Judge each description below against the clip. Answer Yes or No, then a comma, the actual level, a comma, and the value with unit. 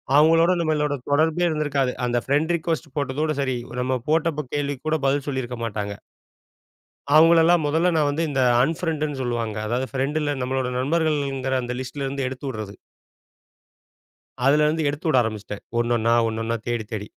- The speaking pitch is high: No, medium, 140 Hz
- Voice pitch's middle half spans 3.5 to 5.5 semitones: Yes, average, 3.8 semitones